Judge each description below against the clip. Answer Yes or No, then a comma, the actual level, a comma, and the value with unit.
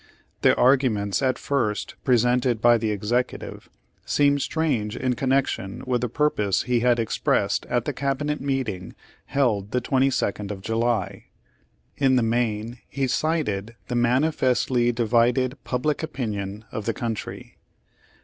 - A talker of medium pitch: No, low, 120 Hz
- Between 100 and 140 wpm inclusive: Yes, slow, 135 wpm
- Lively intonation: No, average, 3.2 semitones